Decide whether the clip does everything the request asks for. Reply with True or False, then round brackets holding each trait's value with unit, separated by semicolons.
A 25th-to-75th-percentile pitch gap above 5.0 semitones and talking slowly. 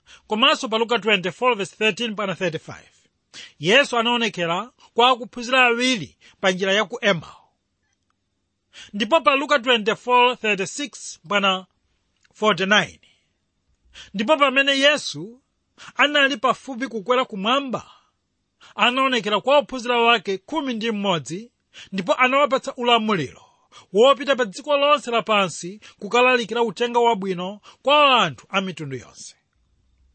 True (5.4 semitones; 90 wpm)